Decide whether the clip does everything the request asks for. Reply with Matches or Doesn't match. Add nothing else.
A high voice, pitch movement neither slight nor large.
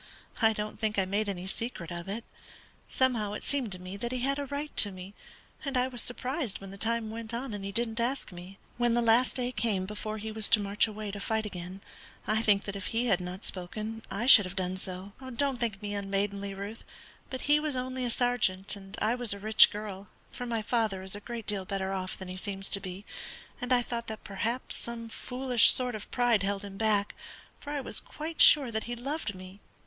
Matches